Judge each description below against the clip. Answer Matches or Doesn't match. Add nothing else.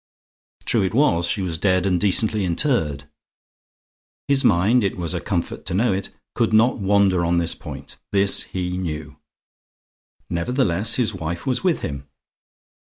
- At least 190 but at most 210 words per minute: Doesn't match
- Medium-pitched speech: Doesn't match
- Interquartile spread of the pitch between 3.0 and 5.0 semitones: Matches